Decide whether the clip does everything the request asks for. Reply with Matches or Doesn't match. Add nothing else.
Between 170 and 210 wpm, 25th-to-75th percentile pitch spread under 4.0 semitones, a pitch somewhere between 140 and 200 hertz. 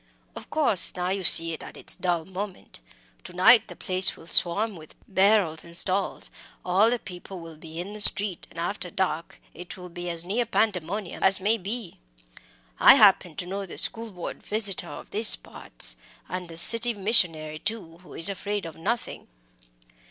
Matches